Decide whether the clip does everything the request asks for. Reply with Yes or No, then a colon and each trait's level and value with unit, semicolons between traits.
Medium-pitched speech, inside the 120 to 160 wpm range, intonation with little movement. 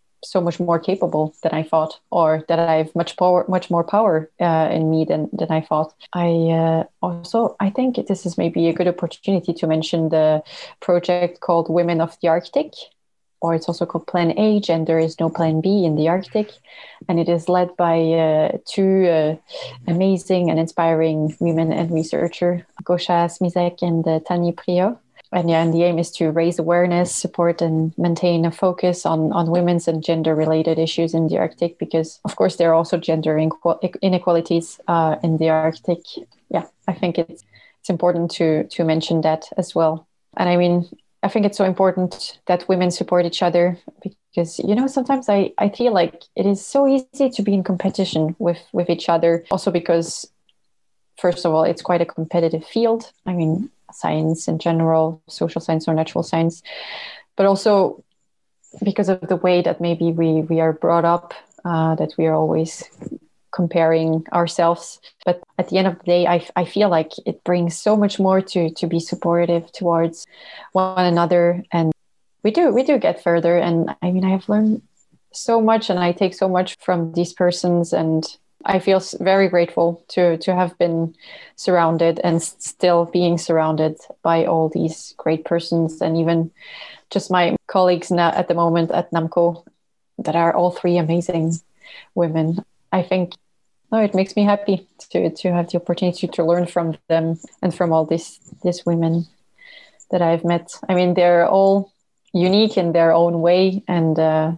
No: medium, 170 Hz; average, 180 wpm; narrow, 1.9 semitones